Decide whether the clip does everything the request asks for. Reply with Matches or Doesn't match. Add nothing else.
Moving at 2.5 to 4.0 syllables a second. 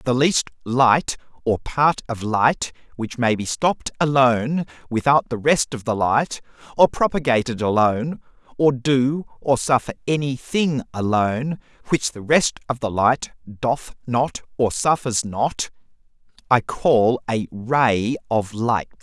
Matches